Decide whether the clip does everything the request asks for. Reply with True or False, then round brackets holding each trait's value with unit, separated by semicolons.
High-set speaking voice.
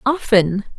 True (225 Hz)